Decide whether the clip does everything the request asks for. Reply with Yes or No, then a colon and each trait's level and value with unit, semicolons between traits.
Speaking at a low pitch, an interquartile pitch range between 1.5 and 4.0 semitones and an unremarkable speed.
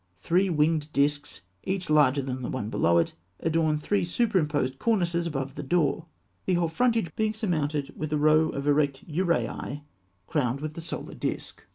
No: medium, 155 Hz; average, 3.3 semitones; average, 170 wpm